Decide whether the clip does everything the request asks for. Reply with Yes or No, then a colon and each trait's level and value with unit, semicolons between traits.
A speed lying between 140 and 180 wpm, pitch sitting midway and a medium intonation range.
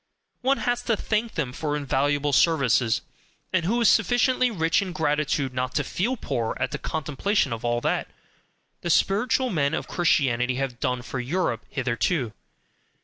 No: average, 160 wpm; medium, 145 Hz; wide, 7.5 semitones